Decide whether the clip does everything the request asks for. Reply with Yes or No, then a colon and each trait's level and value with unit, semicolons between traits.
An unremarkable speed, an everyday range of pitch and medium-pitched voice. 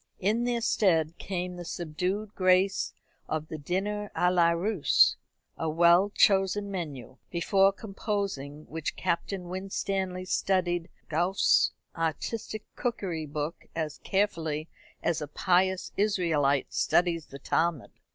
No: slow, 120 wpm; average, 3.4 semitones; medium, 180 Hz